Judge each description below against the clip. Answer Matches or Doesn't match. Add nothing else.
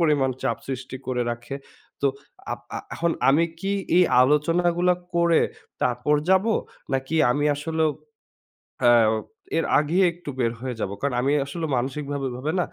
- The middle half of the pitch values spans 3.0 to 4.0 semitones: Doesn't match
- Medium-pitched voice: Matches